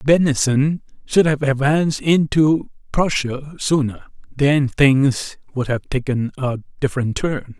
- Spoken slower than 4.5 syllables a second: Yes, 4.1 syllables/s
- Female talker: No, male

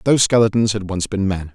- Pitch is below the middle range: Yes, low, 105 Hz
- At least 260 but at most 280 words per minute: No, fast, 235 wpm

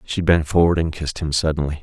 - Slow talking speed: No, fast, 230 wpm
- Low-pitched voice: Yes, very low, 80 Hz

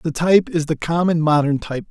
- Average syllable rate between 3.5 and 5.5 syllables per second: No, 6.2 syllables/s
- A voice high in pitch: No, medium, 160 Hz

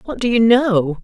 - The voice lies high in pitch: Yes, high, 220 Hz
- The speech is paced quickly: Yes, fast, 230 wpm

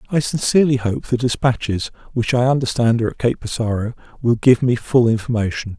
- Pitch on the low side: Yes, low, 120 Hz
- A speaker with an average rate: Yes, average, 175 wpm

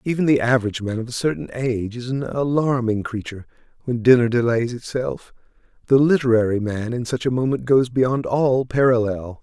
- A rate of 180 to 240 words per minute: No, average, 170 wpm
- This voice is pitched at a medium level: No, low, 125 Hz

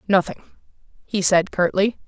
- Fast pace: No, slow, 115 wpm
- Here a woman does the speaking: Yes, female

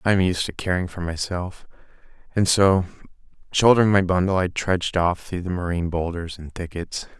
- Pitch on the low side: Yes, very low, 90 Hz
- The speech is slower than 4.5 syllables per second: No, 5.5 syllables/s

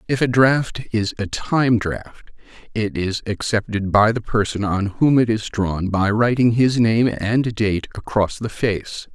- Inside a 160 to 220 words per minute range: Yes, average, 175 wpm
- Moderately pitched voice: No, low, 110 Hz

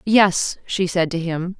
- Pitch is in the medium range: Yes, medium, 180 Hz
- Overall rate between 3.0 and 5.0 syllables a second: Yes, 3.6 syllables/s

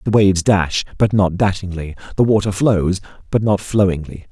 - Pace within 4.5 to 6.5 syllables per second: Yes, 5.1 syllables/s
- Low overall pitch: Yes, very low, 95 Hz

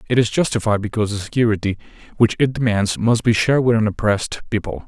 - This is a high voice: No, low, 110 Hz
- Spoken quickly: No, average, 195 wpm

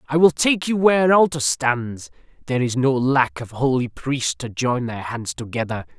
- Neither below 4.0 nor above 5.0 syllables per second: Yes, 4.8 syllables/s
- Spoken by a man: Yes, male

